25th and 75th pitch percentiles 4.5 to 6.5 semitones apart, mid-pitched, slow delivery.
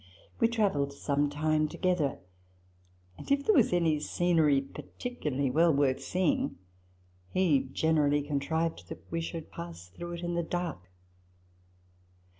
No: average, 3.8 semitones; medium, 155 Hz; slow, 130 wpm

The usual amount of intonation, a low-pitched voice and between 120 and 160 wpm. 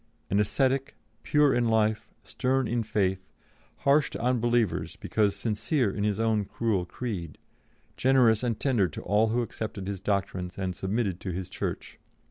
Yes: average, 3.7 semitones; low, 110 Hz; average, 155 wpm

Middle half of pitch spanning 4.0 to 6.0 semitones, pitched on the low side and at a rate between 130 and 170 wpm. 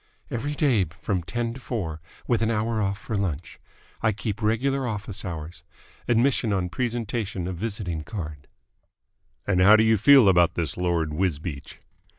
Yes: average, 4.7 semitones; low, 100 Hz; average, 160 wpm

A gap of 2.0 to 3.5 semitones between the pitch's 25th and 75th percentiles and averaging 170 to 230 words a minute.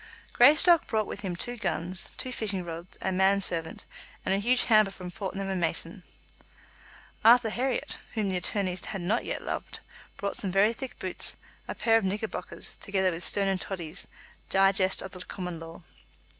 Yes: average, 3.1 semitones; average, 175 wpm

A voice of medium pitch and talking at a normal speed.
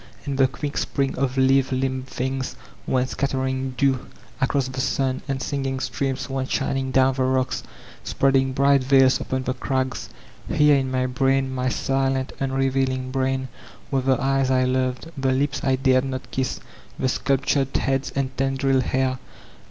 No: low, 130 Hz; average, 160 wpm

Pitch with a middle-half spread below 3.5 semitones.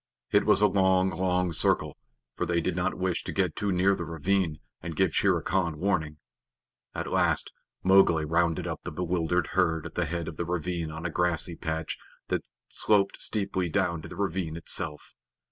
Yes: narrow, 2.4 semitones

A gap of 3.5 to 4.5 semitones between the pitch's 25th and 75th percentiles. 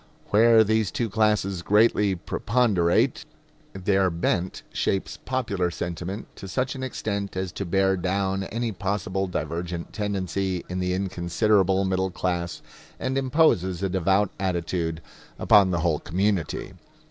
No: narrow, 2.5 semitones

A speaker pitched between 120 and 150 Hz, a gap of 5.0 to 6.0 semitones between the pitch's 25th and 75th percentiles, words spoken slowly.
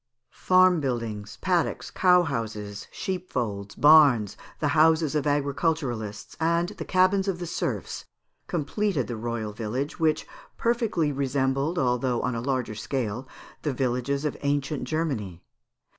Yes: medium, 140 Hz; wide, 5.6 semitones; slow, 130 wpm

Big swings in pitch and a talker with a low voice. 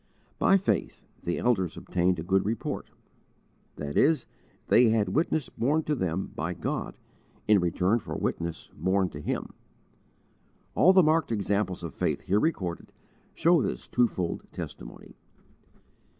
Yes: wide, 7.2 semitones; low, 100 Hz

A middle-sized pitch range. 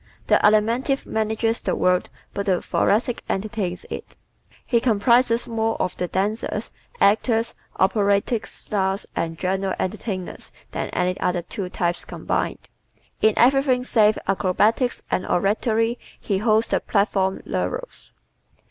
Yes: average, 3.2 semitones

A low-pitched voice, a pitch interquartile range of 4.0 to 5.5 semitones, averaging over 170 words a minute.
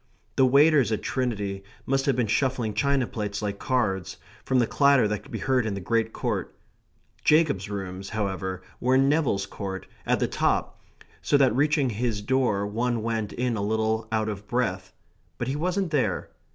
Yes: low, 115 Hz; average, 4.4 semitones; average, 180 wpm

